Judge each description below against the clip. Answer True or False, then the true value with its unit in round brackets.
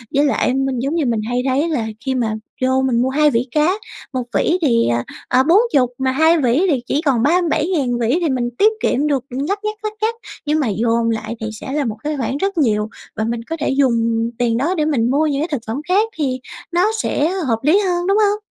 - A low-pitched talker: False (270 Hz)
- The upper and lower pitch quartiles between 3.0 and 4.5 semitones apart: False (5.2 semitones)